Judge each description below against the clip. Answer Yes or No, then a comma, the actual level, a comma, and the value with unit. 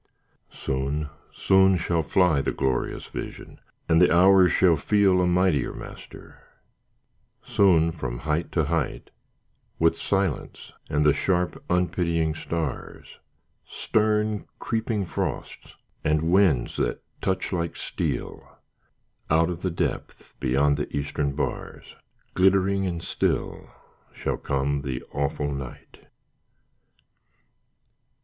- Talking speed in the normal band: No, slow, 110 wpm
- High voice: No, very low, 85 Hz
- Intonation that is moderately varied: Yes, average, 4.3 semitones